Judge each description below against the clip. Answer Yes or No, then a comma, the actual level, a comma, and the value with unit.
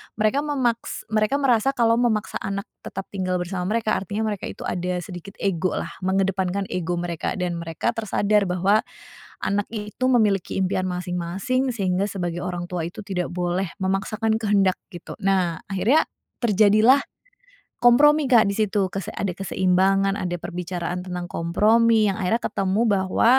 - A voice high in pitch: Yes, high, 195 Hz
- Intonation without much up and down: No, average, 3.2 semitones